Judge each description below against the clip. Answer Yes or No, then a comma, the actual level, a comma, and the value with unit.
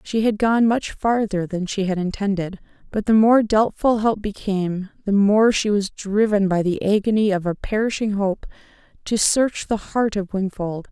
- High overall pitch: Yes, high, 205 Hz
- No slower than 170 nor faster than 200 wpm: Yes, average, 180 wpm